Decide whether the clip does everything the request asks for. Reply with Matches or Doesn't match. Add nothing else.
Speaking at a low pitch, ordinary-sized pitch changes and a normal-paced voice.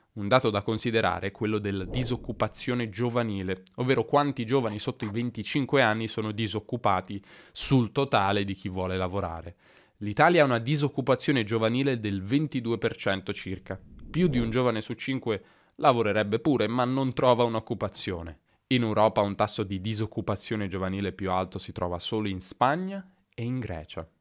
Matches